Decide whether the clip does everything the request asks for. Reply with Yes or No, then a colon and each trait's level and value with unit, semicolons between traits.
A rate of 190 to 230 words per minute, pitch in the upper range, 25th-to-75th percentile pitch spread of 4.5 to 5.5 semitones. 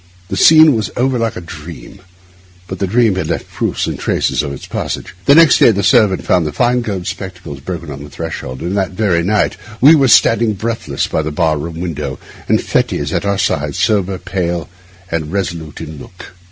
No: fast, 205 wpm; very low, 95 Hz; average, 5.2 semitones